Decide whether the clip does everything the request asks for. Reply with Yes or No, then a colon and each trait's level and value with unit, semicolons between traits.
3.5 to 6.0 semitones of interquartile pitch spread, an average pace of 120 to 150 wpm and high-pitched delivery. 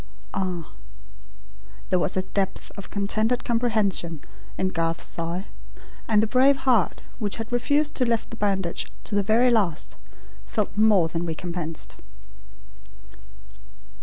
Yes: average, 5.0 semitones; slow, 135 wpm; high, 200 Hz